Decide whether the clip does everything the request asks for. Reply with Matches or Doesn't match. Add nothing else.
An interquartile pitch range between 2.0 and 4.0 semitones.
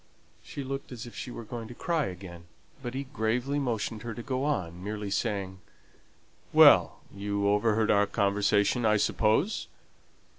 Matches